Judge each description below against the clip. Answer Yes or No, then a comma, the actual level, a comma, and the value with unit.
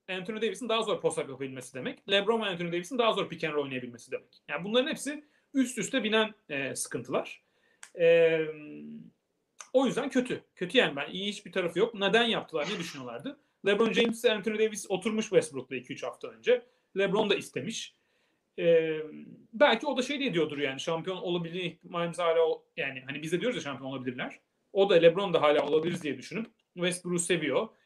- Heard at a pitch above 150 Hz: Yes, high, 190 Hz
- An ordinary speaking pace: No, fast, 175 wpm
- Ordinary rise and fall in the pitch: No, wide, 6.2 semitones